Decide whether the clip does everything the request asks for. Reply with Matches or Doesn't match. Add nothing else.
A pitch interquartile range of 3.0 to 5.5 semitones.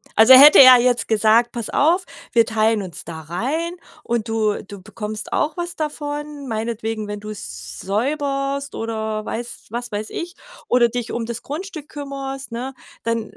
Matches